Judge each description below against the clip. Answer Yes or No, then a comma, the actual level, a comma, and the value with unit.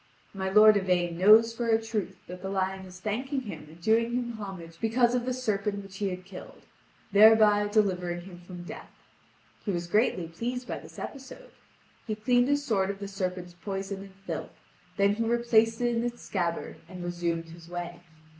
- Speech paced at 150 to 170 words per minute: No, average, 190 wpm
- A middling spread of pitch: Yes, average, 4.0 semitones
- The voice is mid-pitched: No, high, 200 Hz